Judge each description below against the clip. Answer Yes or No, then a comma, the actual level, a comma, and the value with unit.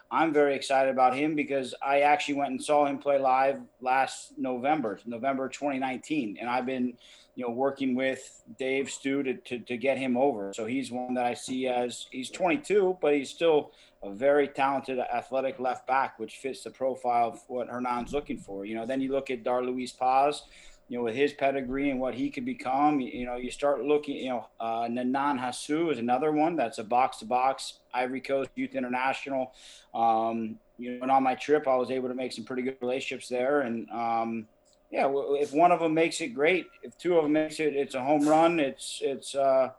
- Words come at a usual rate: No, fast, 215 wpm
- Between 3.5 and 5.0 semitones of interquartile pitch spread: No, narrow, 2.4 semitones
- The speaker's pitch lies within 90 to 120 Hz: No, low, 130 Hz